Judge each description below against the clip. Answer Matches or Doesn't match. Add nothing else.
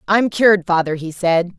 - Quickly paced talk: Doesn't match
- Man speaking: Doesn't match